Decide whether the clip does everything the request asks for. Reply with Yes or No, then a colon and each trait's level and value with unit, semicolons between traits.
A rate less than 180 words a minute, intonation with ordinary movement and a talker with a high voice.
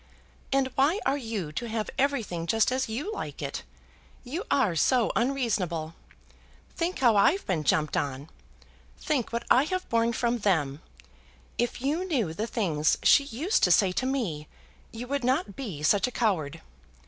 No: average, 165 wpm; wide, 7.1 semitones; high, 230 Hz